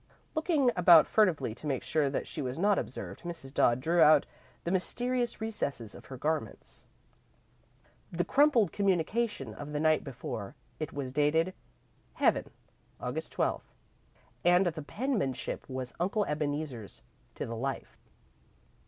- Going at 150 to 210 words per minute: No, average, 140 wpm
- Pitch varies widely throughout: Yes, wide, 6.3 semitones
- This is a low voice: No, medium, 155 Hz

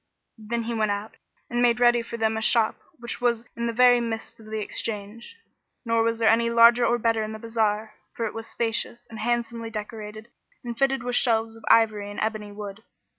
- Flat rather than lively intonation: Yes, narrow, 1.4 semitones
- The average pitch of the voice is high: Yes, high, 225 Hz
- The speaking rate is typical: No, fast, 210 wpm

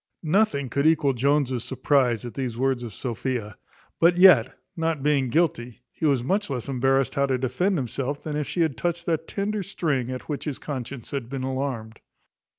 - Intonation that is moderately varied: Yes, average, 3.8 semitones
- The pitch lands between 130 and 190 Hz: Yes, low, 135 Hz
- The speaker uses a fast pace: No, average, 185 wpm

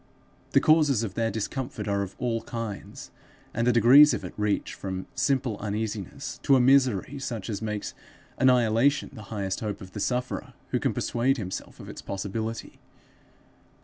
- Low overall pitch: Yes, low, 115 Hz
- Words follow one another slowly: No, average, 165 wpm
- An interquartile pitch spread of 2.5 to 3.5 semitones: No, average, 3.9 semitones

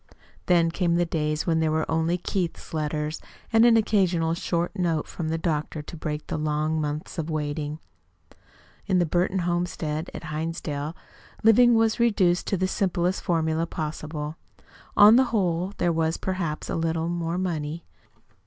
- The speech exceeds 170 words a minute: No, average, 160 wpm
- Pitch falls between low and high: Yes, medium, 165 Hz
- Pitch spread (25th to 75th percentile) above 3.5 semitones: No, narrow, 2.5 semitones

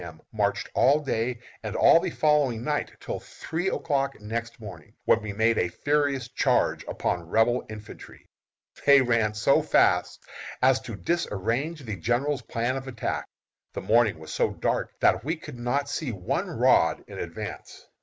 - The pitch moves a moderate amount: Yes, average, 4.6 semitones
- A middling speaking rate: Yes, average, 165 wpm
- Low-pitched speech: Yes, low, 120 Hz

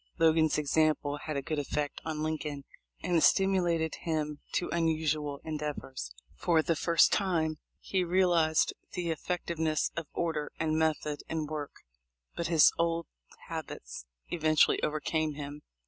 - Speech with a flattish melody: Yes, narrow, 1.8 semitones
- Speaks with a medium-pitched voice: Yes, medium, 155 Hz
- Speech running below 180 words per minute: Yes, average, 140 wpm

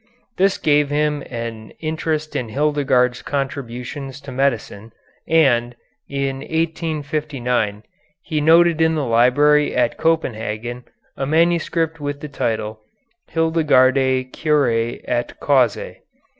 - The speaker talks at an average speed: No, slow, 105 wpm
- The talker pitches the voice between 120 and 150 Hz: Yes, medium, 140 Hz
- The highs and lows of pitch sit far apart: No, average, 4.0 semitones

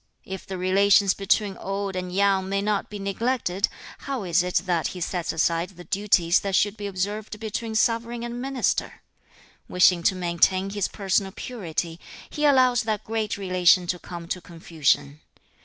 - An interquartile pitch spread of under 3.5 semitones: Yes, average, 2.9 semitones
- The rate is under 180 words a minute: Yes, average, 165 wpm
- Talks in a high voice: Yes, high, 195 Hz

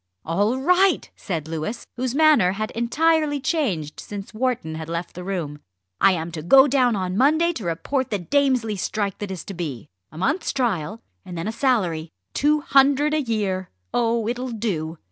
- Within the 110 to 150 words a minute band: No, average, 180 wpm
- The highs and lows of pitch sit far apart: Yes, wide, 7.2 semitones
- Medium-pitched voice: No, high, 220 Hz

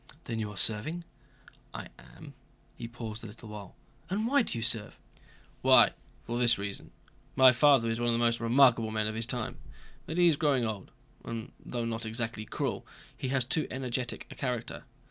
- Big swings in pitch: No, narrow, 2.5 semitones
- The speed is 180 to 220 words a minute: Yes, average, 190 wpm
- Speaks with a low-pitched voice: Yes, low, 120 Hz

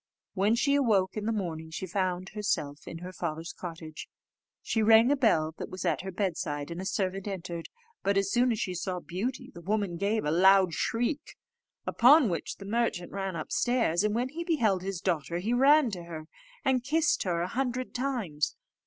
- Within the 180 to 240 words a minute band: Yes, average, 195 wpm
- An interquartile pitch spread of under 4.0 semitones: No, wide, 5.4 semitones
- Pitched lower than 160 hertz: No, high, 195 Hz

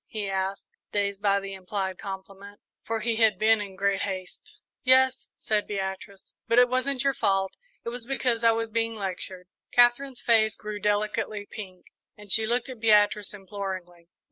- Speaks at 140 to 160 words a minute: No, average, 170 wpm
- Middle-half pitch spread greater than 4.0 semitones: No, average, 2.9 semitones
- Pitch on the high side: Yes, high, 210 Hz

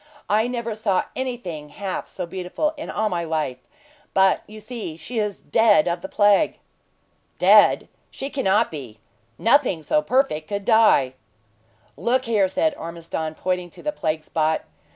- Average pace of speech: Yes, average, 150 wpm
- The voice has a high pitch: Yes, high, 195 Hz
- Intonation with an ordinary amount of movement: No, wide, 6.1 semitones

